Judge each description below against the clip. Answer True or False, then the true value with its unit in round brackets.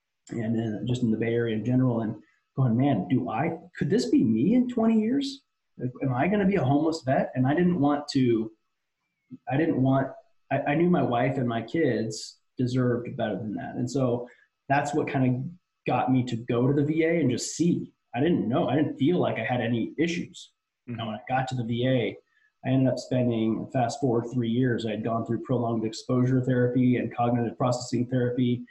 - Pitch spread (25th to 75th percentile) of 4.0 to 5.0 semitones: False (3.3 semitones)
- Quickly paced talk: True (215 wpm)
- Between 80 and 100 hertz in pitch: False (125 Hz)